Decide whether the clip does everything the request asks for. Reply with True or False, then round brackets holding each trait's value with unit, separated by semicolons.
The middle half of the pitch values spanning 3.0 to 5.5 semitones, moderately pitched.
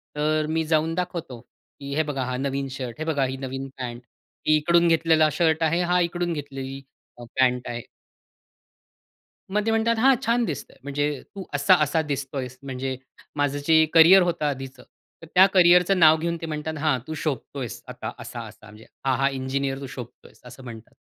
True (3.8 semitones; 150 Hz)